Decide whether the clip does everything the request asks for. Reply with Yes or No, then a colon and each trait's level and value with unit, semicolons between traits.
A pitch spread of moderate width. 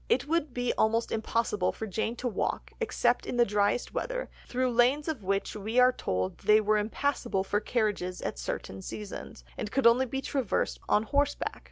Yes: average, 3.7 semitones